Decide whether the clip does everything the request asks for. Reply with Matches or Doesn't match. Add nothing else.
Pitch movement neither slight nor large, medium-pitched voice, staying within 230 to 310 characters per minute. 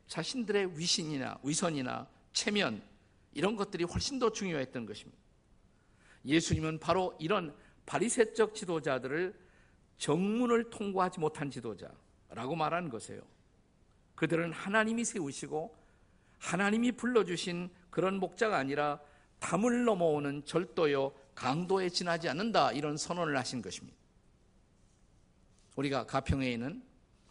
Doesn't match